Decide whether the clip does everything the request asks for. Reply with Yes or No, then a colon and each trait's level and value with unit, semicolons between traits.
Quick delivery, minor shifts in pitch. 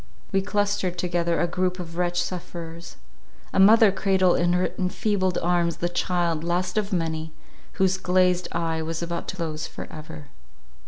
No: average, 160 wpm; narrow, 1.8 semitones